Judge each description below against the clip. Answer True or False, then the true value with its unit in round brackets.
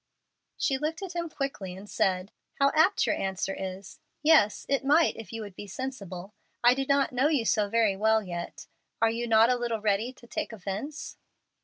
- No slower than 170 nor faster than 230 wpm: True (195 wpm)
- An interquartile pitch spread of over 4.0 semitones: True (5.6 semitones)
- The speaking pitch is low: False (225 Hz)